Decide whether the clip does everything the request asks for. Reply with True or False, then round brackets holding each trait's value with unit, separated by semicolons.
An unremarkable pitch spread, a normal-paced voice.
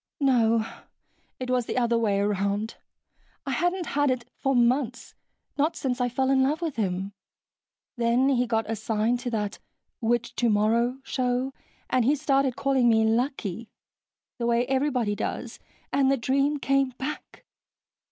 True (3.1 semitones; 150 wpm)